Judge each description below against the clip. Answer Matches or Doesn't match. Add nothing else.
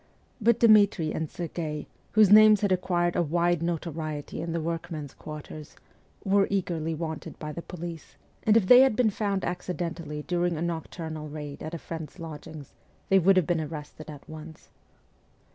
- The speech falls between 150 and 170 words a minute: Matches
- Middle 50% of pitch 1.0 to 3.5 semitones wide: Matches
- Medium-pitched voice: Matches